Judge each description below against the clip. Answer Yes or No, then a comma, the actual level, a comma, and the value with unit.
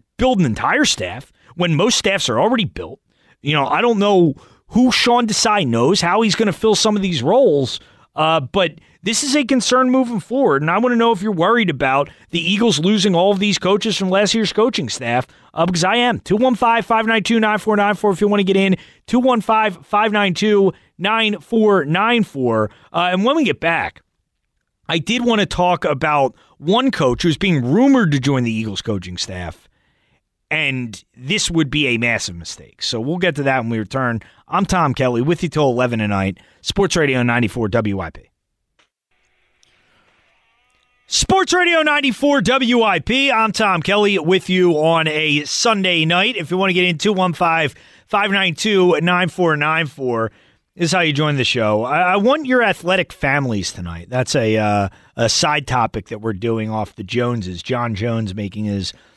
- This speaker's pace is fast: No, average, 175 wpm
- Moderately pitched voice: Yes, medium, 175 Hz